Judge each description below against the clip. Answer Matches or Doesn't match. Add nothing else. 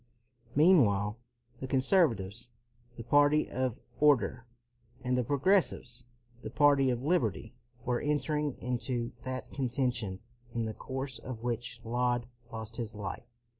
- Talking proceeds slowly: Matches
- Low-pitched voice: Matches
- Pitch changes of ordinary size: Matches